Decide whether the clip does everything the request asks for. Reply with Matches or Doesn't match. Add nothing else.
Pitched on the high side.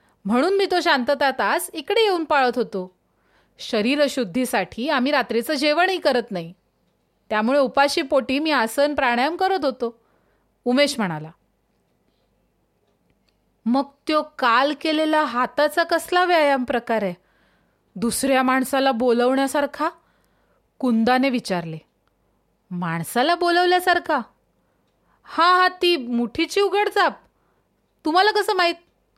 Matches